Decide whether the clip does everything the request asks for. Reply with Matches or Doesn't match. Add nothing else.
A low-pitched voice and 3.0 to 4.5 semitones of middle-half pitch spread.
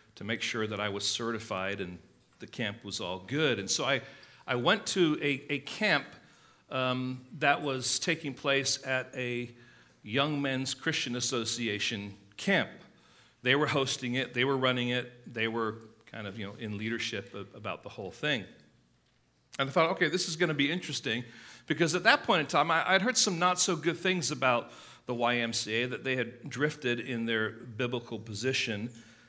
Matches